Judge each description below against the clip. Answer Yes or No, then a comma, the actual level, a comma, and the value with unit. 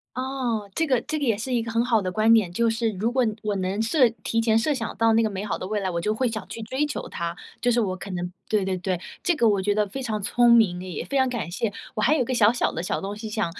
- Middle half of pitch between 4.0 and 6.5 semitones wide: No, average, 3.3 semitones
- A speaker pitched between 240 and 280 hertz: No, high, 225 Hz